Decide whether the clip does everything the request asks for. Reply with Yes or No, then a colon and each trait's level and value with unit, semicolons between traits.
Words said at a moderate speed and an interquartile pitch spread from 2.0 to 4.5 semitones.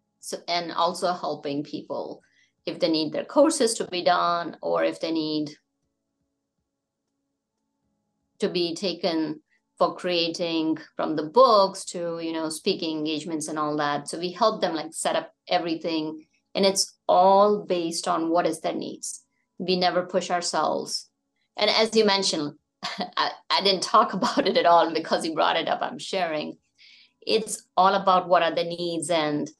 Yes: average, 165 wpm; average, 3.2 semitones